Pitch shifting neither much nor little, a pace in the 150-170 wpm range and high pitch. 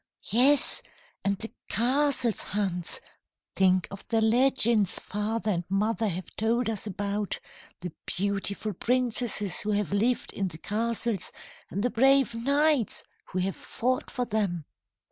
No: average, 3.3 semitones; slow, 135 wpm; high, 215 Hz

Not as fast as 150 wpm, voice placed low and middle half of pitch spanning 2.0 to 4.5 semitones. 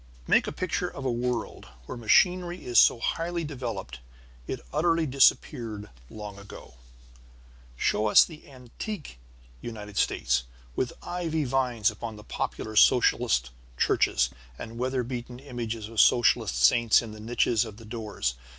Yes: average, 140 wpm; low, 120 Hz; average, 3.8 semitones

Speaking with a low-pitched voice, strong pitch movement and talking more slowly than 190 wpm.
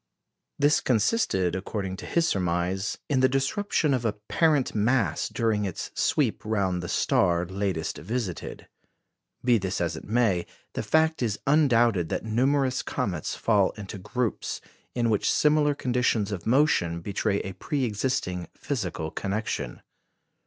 Yes: low, 110 Hz; wide, 5.7 semitones; average, 140 wpm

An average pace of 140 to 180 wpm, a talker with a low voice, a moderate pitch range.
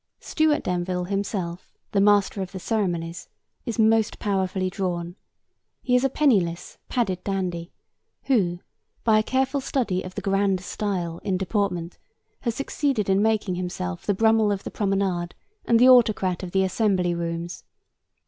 No: average, 150 wpm; high, 195 Hz; average, 3.5 semitones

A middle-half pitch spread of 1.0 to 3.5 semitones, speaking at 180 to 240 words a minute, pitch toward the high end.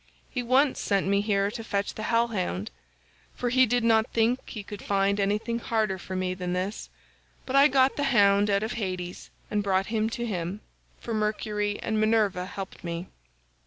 Yes: average, 2.8 semitones; average, 185 wpm; high, 210 Hz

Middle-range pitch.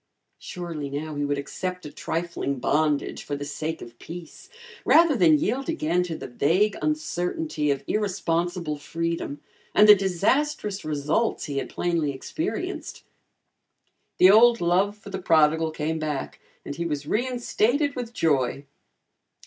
Yes: medium, 170 Hz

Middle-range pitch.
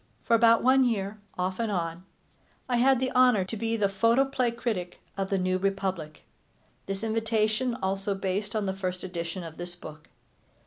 No: high, 200 Hz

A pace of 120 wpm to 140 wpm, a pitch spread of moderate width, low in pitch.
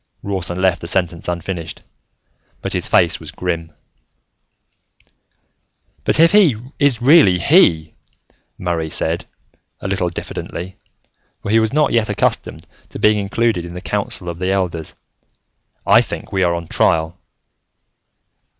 Yes: slow, 135 wpm; average, 4.0 semitones; very low, 90 Hz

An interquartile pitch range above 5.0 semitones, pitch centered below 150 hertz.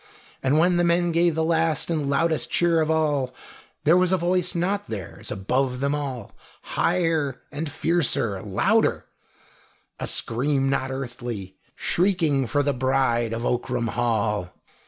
Yes: wide, 5.4 semitones; medium, 140 Hz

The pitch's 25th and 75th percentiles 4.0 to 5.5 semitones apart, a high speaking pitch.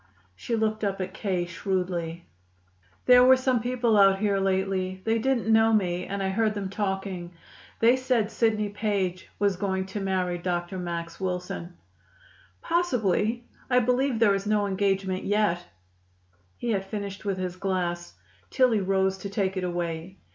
No: average, 2.8 semitones; high, 195 Hz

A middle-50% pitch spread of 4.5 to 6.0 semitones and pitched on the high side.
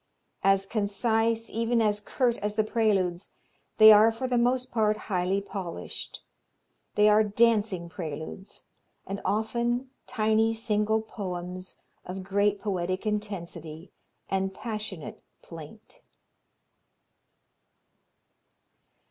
No: average, 2.8 semitones; high, 210 Hz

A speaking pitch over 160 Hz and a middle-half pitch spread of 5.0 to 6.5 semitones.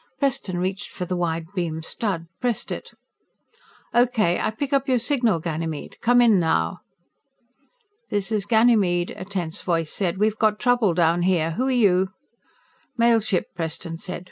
Yes: high, 190 Hz; wide, 5.4 semitones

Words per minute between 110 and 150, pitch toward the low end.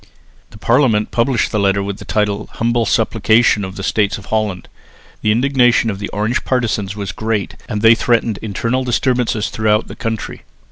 No: average, 175 wpm; low, 110 Hz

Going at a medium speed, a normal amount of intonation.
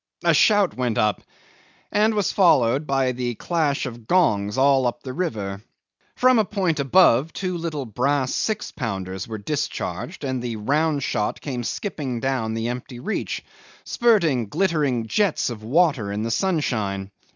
No: average, 155 wpm; wide, 6.7 semitones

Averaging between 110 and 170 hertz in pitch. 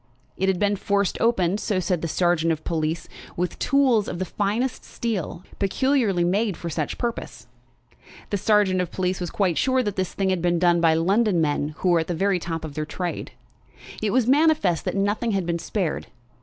No: medium, 185 Hz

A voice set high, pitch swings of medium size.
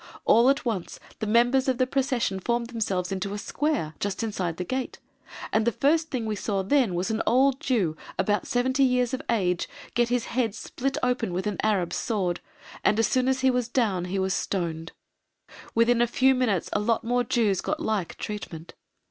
Yes: high, 230 Hz; average, 4.6 semitones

